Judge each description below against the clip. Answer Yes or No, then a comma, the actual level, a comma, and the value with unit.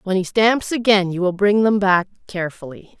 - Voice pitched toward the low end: No, high, 195 Hz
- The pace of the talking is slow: No, average, 200 wpm